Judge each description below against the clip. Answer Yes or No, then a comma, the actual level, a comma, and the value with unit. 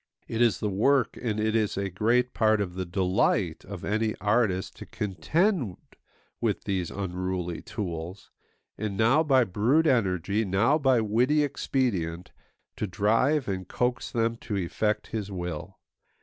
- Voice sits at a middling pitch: No, low, 105 Hz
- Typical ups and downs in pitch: Yes, average, 4.4 semitones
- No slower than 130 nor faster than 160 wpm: Yes, average, 150 wpm